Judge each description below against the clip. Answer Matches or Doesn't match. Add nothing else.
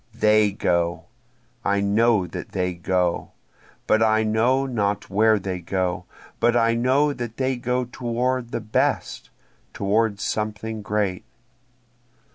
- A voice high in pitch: Doesn't match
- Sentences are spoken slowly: Matches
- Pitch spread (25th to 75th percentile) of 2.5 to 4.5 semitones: Matches